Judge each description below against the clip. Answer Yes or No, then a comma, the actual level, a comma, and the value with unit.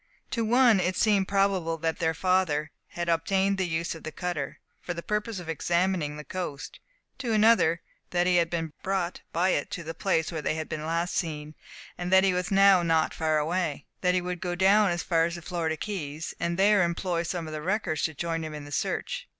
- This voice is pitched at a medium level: Yes, medium, 175 Hz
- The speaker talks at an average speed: No, fast, 230 wpm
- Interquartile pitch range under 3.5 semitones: Yes, average, 2.8 semitones